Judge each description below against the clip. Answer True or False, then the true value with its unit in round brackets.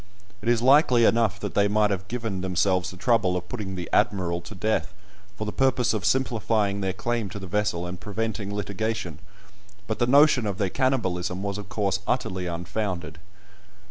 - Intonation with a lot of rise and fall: False (3.4 semitones)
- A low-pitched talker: True (100 Hz)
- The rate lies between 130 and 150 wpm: False (180 wpm)